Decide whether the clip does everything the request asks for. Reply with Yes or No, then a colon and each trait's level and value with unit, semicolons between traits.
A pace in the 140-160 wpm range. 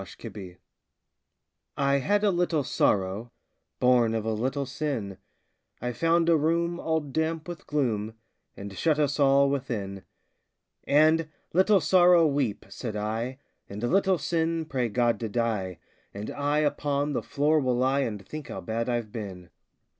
Yes: average, 155 wpm